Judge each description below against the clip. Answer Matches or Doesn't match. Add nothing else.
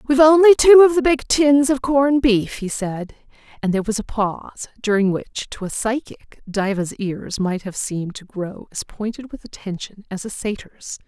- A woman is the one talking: Matches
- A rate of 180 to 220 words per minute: Matches